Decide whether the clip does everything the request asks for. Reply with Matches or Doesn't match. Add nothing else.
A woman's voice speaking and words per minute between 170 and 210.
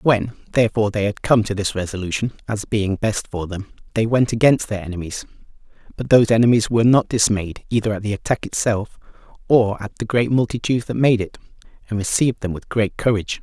Doesn't match